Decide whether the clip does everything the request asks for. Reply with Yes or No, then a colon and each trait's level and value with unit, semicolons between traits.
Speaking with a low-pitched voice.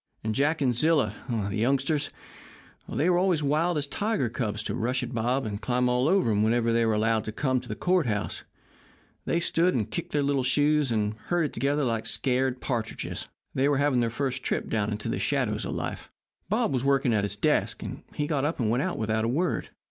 Yes: low, 130 Hz